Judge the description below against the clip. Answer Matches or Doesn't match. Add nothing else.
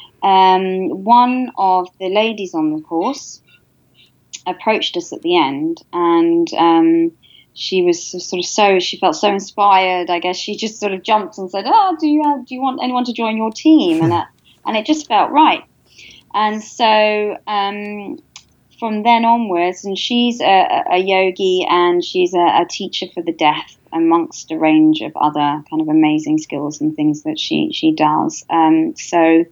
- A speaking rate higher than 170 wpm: Matches